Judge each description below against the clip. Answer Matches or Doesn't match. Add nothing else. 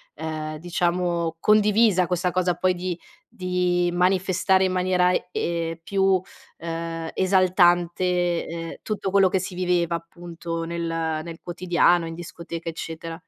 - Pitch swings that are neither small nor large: Doesn't match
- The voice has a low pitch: Doesn't match